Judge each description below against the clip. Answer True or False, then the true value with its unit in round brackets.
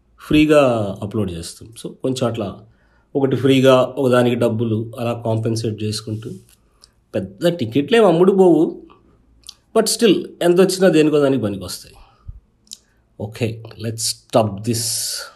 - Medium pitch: False (120 Hz)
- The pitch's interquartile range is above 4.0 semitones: True (4.8 semitones)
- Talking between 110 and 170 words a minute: True (115 wpm)